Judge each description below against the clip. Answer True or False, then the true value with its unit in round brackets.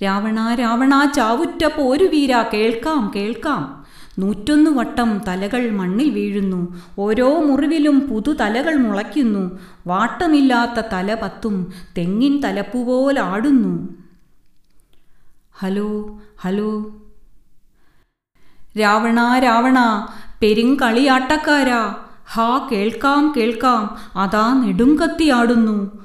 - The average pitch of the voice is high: True (230 Hz)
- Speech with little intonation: False (4.3 semitones)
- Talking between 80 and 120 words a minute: False (70 wpm)